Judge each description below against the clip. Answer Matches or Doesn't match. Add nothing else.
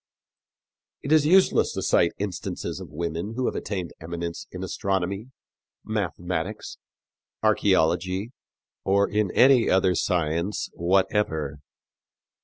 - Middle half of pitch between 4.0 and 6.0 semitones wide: Doesn't match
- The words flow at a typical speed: Doesn't match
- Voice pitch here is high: Doesn't match